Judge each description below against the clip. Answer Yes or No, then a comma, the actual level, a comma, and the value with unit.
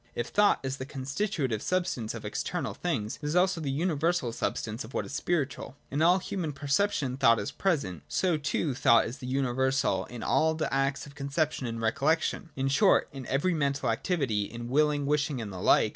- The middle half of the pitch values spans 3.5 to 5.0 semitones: Yes, average, 4.5 semitones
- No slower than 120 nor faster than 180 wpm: No, average, 195 wpm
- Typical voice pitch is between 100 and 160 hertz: Yes, medium, 140 Hz